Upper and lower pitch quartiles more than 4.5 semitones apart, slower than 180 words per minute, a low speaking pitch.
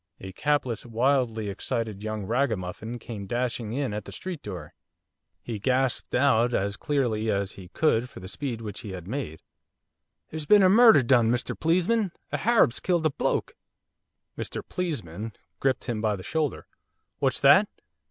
Yes: average, 5.2 semitones; average, 160 wpm; low, 120 Hz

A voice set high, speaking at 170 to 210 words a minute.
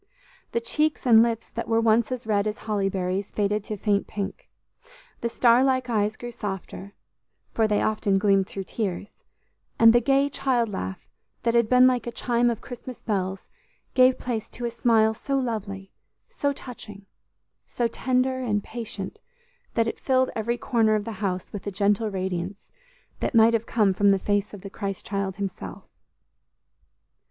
Yes: high, 220 Hz; average, 175 wpm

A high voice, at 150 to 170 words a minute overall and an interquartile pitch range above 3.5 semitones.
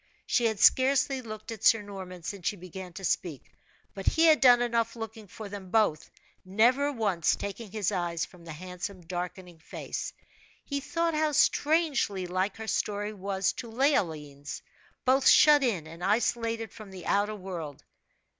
Yes: high, 205 Hz; average, 165 wpm; average, 4.6 semitones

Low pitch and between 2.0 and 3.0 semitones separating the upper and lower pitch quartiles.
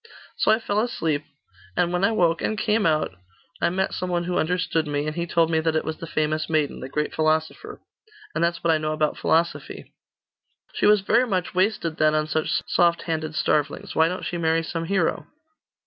No: medium, 165 Hz; narrow, 2.5 semitones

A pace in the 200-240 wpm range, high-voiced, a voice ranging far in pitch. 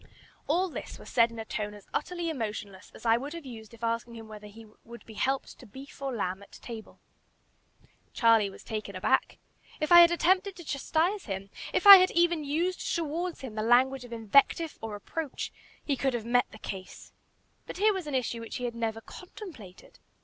Yes: fast, 205 wpm; high, 245 Hz; wide, 6.7 semitones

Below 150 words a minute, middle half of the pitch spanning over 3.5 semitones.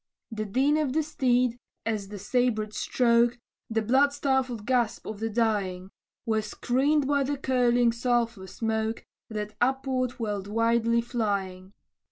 No: average, 140 wpm; average, 3.0 semitones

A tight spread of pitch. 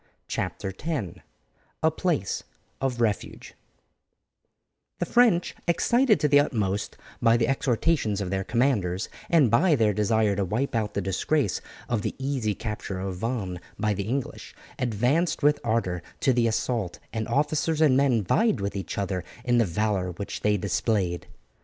No: wide, 5.6 semitones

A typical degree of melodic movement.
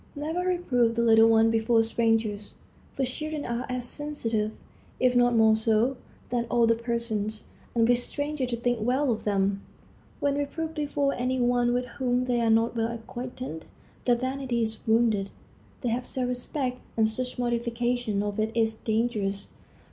No: narrow, 2.0 semitones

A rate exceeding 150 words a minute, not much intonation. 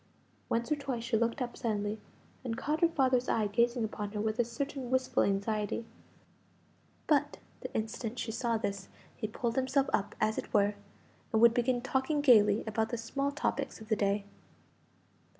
No: average, 175 wpm; average, 3.3 semitones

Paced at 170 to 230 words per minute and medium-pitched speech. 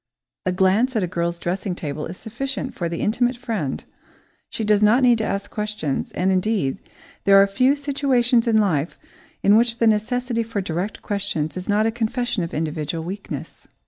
No: average, 180 wpm; high, 210 Hz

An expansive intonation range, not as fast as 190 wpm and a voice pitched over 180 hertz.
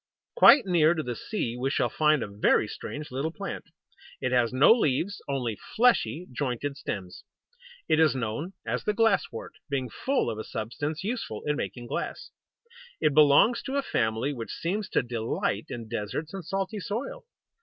No: wide, 8.2 semitones; average, 175 wpm; medium, 145 Hz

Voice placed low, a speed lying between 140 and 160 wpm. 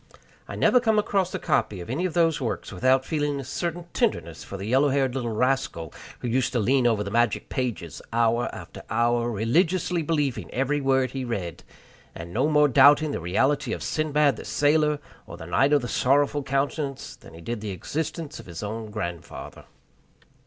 No: low, 130 Hz; average, 190 wpm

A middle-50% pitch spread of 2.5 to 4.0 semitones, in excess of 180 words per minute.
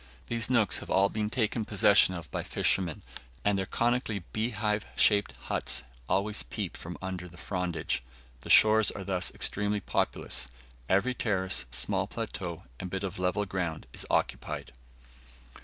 No: average, 2.8 semitones; average, 150 wpm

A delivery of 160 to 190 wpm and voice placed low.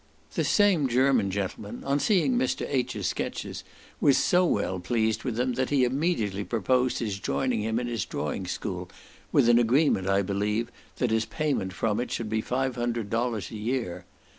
Yes: average, 180 wpm; low, 120 Hz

